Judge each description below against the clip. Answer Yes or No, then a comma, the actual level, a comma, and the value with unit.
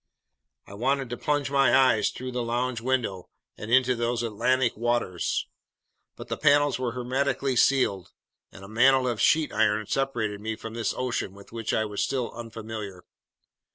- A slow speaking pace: No, average, 165 wpm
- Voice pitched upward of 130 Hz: No, low, 120 Hz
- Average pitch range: Yes, average, 3.0 semitones